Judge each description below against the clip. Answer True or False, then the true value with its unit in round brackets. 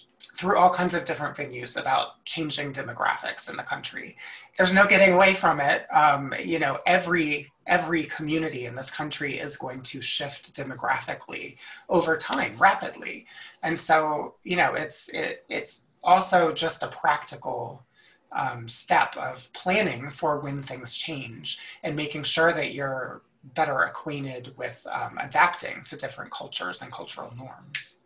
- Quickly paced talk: False (150 wpm)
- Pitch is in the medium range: True (150 Hz)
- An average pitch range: True (3.6 semitones)